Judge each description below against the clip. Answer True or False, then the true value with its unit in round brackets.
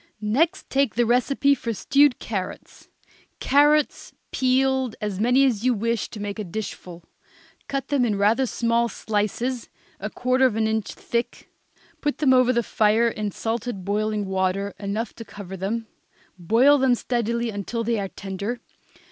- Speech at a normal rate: True (155 wpm)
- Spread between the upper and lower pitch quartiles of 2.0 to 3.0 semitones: False (3.6 semitones)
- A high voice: True (230 Hz)